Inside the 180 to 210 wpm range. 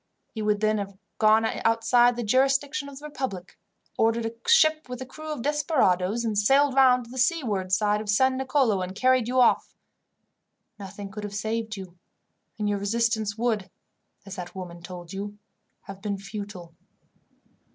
No: average, 165 wpm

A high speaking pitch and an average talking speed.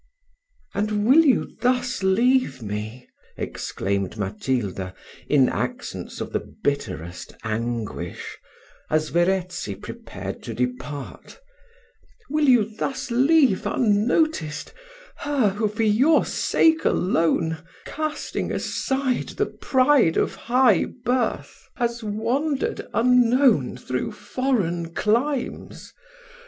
No: high, 210 Hz; slow, 95 wpm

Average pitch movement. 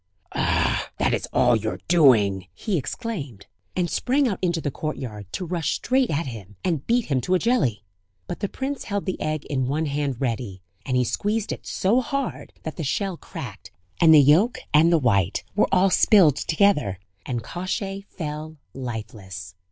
No: wide, 7.9 semitones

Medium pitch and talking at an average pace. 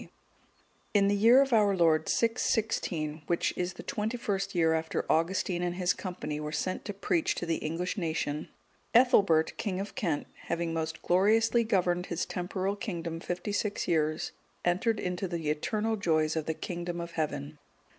Yes: medium, 175 Hz; average, 170 wpm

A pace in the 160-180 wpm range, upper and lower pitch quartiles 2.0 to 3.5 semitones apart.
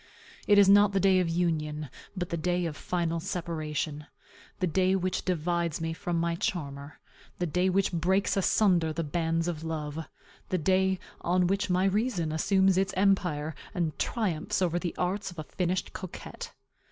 Yes: average, 170 wpm; average, 2.7 semitones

